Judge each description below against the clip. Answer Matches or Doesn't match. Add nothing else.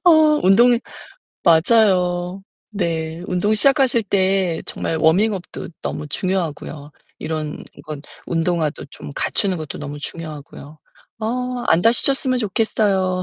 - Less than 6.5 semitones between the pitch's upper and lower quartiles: Matches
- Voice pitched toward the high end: Doesn't match